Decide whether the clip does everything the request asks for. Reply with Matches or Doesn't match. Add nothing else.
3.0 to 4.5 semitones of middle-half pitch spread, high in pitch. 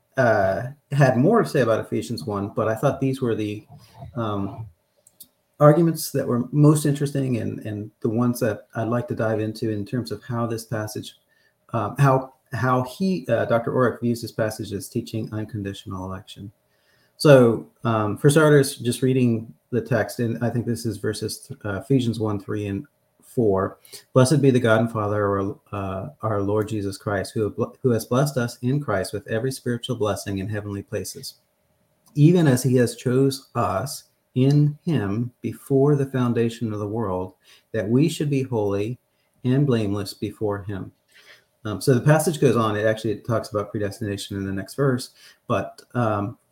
Doesn't match